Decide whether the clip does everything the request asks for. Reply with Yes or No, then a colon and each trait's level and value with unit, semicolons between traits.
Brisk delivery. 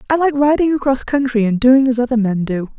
Yes: fast, 235 wpm